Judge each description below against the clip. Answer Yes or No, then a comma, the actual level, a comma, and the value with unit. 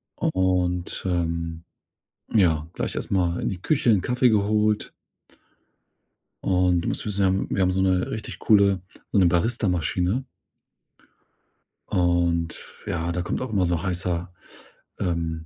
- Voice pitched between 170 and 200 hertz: No, very low, 90 Hz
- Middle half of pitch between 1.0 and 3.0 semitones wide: Yes, narrow, 2.5 semitones